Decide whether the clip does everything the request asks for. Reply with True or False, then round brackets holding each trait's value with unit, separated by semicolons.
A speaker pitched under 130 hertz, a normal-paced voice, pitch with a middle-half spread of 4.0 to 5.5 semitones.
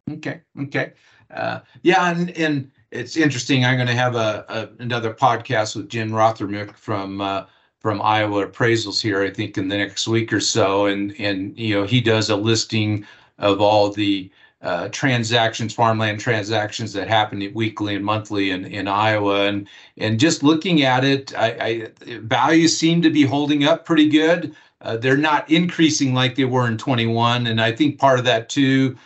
True (115 Hz; 180 wpm; 4.5 semitones)